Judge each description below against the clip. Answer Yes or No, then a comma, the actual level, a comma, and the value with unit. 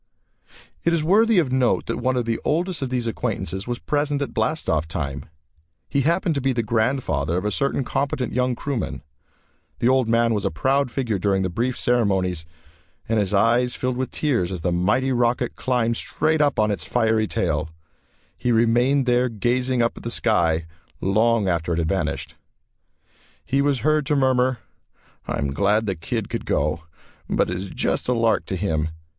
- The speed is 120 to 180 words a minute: No, average, 190 wpm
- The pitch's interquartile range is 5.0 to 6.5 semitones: Yes, average, 5.3 semitones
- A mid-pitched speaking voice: No, low, 120 Hz